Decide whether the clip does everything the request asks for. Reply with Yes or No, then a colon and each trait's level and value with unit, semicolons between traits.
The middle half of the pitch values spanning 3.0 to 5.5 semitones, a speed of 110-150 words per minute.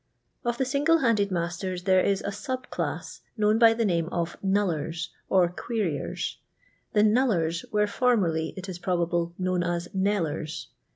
No: average, 3.9 semitones; average, 170 wpm